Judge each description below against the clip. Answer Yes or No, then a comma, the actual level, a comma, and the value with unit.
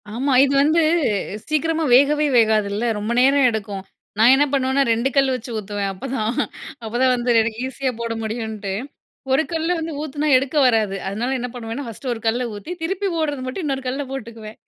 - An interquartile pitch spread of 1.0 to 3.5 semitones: No, average, 4.2 semitones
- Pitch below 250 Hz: No, very high, 255 Hz